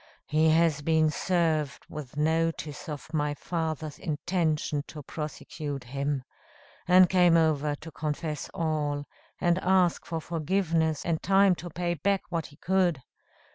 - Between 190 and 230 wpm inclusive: No, slow, 135 wpm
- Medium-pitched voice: Yes, medium, 160 Hz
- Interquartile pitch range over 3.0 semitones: No, narrow, 2.6 semitones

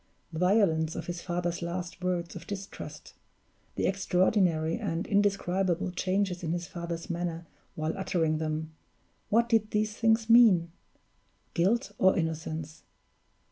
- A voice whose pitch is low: No, medium, 180 Hz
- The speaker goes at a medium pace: No, slow, 130 wpm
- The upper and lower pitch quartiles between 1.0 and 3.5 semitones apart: Yes, average, 3.1 semitones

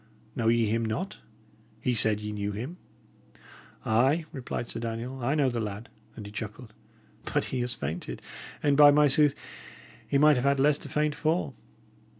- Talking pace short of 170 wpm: No, average, 175 wpm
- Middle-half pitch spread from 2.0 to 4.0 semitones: No, average, 4.7 semitones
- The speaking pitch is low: Yes, low, 125 Hz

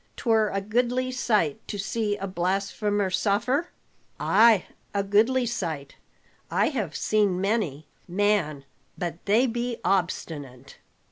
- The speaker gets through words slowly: Yes, slow, 120 wpm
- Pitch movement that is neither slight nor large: Yes, average, 4.2 semitones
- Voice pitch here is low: No, high, 205 Hz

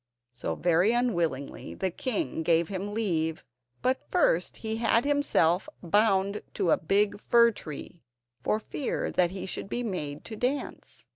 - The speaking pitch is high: Yes, high, 195 Hz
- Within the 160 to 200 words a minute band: No, average, 150 wpm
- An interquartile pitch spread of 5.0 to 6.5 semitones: Yes, average, 5.3 semitones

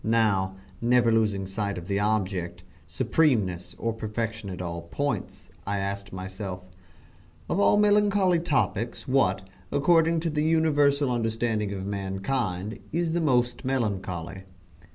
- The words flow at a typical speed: No, slow, 130 wpm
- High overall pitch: No, low, 110 Hz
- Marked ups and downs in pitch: Yes, wide, 6.6 semitones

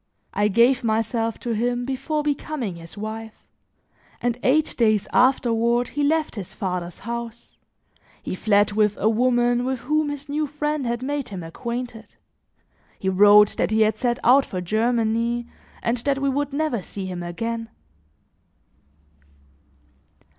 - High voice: Yes, high, 235 Hz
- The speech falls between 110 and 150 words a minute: Yes, average, 145 wpm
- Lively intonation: No, average, 3.5 semitones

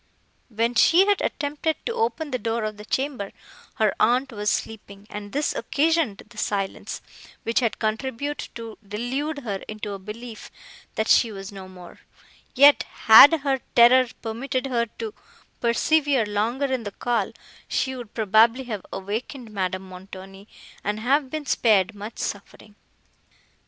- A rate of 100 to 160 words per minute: Yes, average, 150 wpm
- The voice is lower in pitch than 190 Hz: No, high, 230 Hz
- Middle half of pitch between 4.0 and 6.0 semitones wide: Yes, average, 4.4 semitones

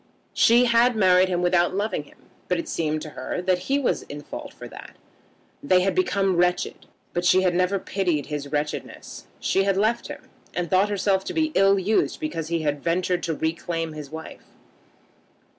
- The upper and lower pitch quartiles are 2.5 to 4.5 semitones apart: Yes, average, 3.3 semitones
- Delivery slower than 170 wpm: No, average, 190 wpm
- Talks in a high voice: No, medium, 180 Hz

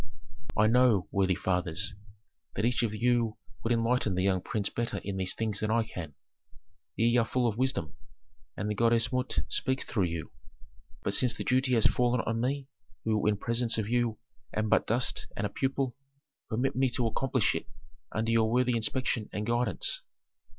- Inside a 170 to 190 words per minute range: Yes, average, 180 wpm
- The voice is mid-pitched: No, low, 115 Hz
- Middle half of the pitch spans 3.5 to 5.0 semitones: No, average, 3.0 semitones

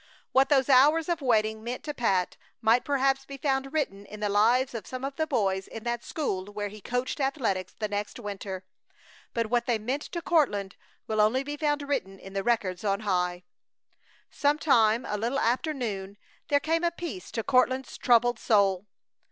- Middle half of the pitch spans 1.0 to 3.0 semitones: No, average, 4.9 semitones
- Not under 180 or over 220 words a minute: Yes, average, 190 wpm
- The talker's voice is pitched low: No, high, 235 Hz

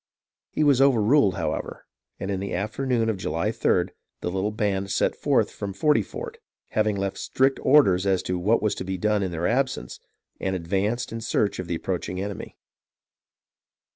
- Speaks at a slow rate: No, average, 175 wpm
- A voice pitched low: Yes, low, 100 Hz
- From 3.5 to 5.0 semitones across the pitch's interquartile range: Yes, average, 4.0 semitones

